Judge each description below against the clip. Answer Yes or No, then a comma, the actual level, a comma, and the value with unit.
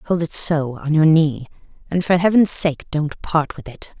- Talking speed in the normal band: No, fast, 210 wpm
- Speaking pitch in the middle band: Yes, medium, 160 Hz